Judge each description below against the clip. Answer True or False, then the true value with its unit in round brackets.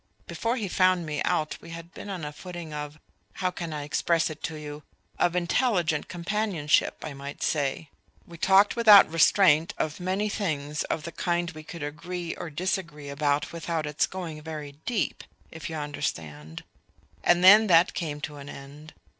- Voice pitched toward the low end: False (165 Hz)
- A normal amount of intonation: True (3.4 semitones)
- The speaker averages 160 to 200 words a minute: True (175 wpm)